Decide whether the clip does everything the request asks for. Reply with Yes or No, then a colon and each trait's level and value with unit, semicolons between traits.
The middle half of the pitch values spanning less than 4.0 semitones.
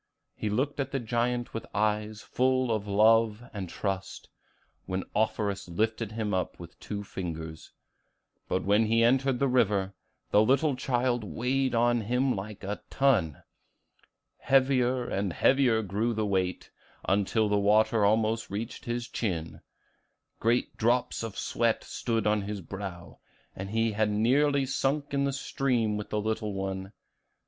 Yes: average, 3.4 semitones